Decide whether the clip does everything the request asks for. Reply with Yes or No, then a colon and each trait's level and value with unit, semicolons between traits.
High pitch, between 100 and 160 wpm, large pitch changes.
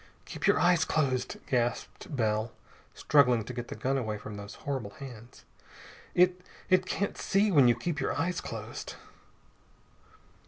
No: low, 130 Hz; average, 150 wpm; wide, 6.6 semitones